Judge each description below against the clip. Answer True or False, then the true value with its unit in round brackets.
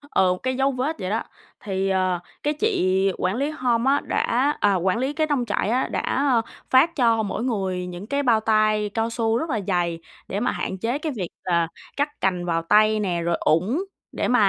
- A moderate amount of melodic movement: False (5.7 semitones)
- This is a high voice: True (220 Hz)